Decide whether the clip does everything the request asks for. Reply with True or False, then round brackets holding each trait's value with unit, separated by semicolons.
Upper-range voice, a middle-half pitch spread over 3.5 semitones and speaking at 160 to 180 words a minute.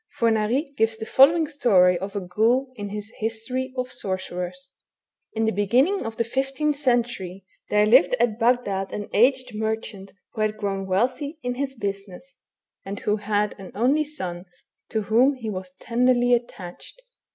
True (225 Hz; 4.1 semitones; 165 wpm)